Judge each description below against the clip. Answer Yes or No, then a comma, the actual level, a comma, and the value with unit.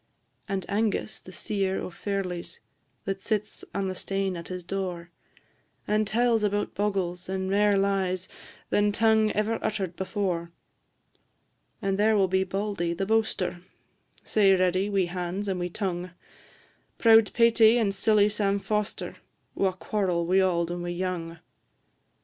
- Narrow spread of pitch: Yes, narrow, 2.3 semitones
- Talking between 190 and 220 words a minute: No, average, 145 wpm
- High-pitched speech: Yes, high, 195 Hz